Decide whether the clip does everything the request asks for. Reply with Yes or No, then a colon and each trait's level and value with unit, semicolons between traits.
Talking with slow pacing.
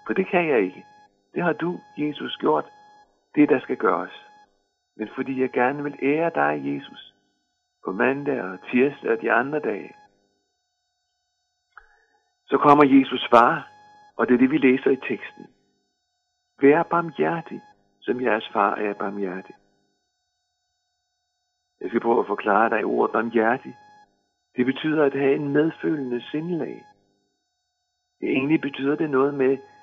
Yes: slow, 140 wpm